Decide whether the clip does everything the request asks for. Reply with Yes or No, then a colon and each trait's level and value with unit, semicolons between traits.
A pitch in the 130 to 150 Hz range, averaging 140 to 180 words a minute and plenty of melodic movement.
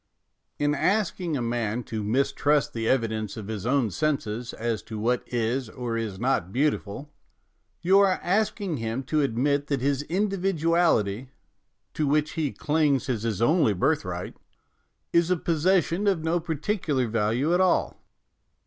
Yes: medium, 140 Hz; average, 155 wpm; wide, 6.2 semitones